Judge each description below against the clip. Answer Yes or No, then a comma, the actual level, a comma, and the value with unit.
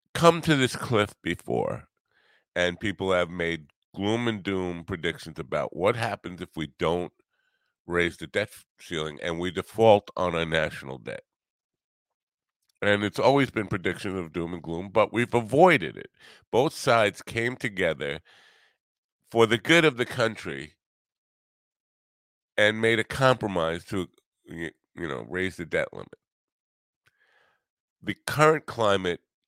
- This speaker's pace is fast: No, slow, 135 wpm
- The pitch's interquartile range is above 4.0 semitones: Yes, average, 5.2 semitones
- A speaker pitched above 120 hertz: No, very low, 95 Hz